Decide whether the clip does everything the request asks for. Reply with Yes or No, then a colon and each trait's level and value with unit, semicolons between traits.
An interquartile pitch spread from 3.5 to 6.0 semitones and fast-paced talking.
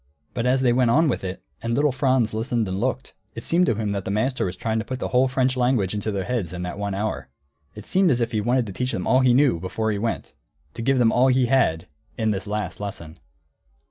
Yes: average, 4.0 semitones; fast, 260 wpm